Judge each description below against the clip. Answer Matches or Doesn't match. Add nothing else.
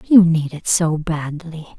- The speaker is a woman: Matches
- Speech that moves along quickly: Doesn't match